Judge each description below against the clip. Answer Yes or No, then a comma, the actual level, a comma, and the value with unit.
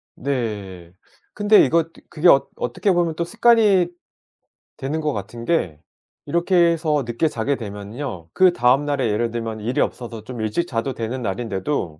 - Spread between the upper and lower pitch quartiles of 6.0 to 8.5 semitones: Yes, wide, 7.1 semitones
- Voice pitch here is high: No, low, 130 Hz